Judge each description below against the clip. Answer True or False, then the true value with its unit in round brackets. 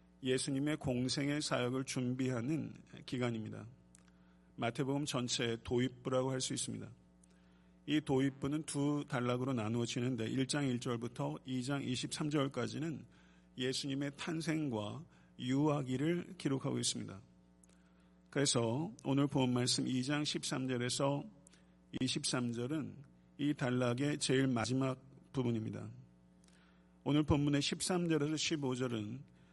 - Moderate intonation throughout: True (4.7 semitones)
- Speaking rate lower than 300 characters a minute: True (240 characters per minute)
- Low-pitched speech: True (130 Hz)